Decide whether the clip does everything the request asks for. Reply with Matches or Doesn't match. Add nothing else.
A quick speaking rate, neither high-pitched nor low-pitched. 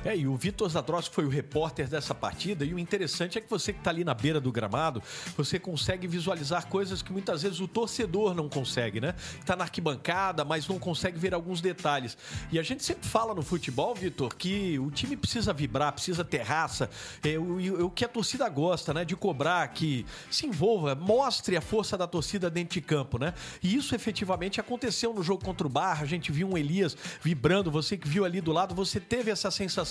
Matches